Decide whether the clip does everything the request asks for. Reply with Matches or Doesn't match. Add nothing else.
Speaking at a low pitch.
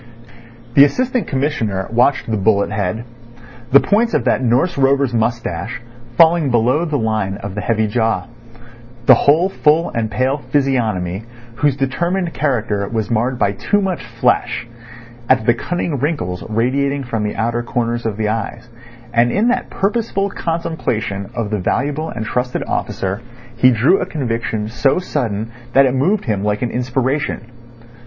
Matches